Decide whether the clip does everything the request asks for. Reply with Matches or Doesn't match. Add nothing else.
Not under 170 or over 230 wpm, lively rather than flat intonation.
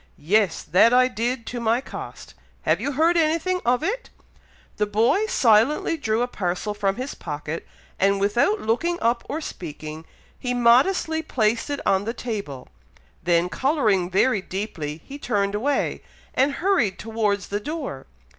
Doesn't match